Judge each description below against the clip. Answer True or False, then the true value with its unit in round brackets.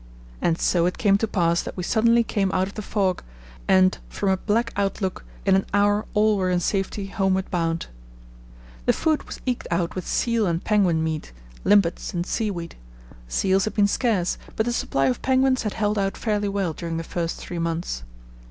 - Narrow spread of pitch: False (3.4 semitones)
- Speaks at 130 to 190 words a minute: False (200 wpm)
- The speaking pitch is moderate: False (195 Hz)